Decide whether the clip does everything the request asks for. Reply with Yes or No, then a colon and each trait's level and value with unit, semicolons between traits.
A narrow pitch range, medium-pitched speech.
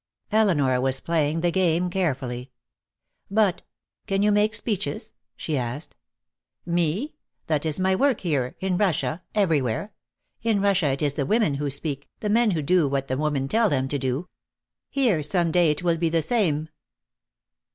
No: wide, 5.4 semitones; medium, 165 Hz